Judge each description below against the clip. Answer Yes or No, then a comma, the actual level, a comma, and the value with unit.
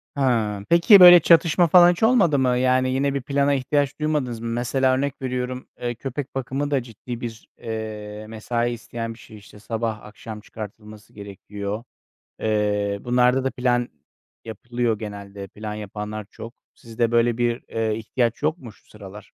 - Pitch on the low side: Yes, low, 120 Hz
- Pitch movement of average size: Yes, average, 3.6 semitones